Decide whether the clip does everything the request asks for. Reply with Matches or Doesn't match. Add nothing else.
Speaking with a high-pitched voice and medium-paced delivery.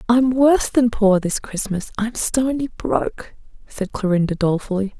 Matches